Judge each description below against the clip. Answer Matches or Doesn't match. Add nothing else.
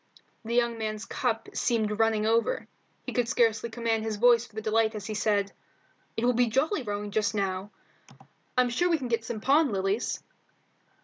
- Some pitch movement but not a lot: Doesn't match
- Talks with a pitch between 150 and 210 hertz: Doesn't match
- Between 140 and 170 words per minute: Doesn't match